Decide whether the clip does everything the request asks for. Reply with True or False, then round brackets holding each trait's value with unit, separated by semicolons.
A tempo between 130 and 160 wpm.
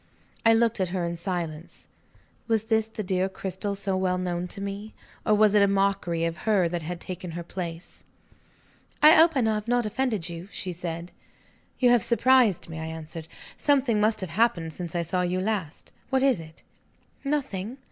False (190 wpm)